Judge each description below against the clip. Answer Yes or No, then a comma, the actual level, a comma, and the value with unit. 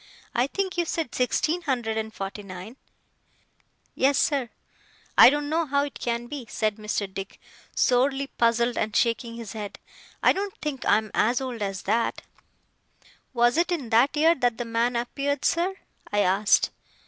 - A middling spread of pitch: Yes, average, 4.5 semitones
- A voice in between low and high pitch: No, high, 240 Hz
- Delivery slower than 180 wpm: Yes, average, 170 wpm